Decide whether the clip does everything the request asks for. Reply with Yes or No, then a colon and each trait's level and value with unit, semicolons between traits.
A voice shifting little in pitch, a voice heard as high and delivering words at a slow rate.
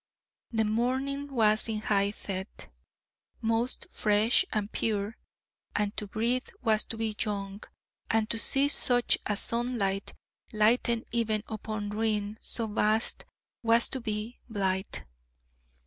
Yes: narrow, 2.0 semitones; high, 220 Hz; slow, 125 wpm